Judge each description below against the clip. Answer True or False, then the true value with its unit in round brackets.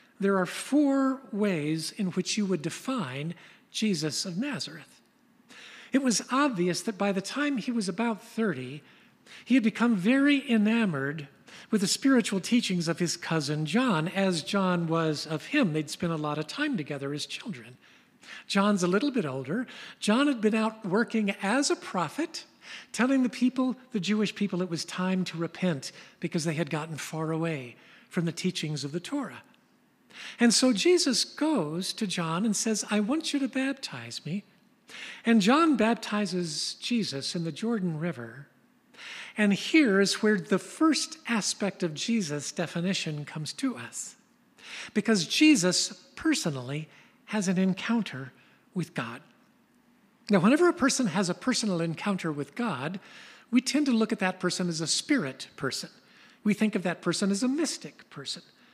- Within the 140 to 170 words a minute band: True (160 wpm)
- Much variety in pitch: True (5.9 semitones)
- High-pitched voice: True (205 Hz)